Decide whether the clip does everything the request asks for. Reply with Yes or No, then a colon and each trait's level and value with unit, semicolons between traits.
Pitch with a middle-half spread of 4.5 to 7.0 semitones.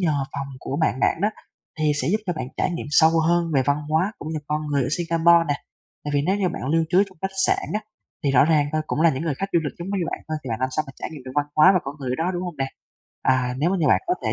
No: average, 3.5 semitones